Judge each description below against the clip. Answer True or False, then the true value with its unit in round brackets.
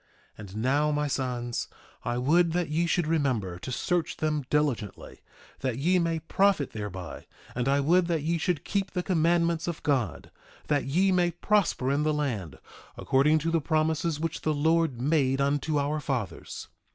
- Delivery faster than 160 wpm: True (175 wpm)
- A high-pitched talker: False (150 Hz)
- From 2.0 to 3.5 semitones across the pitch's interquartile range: False (4.0 semitones)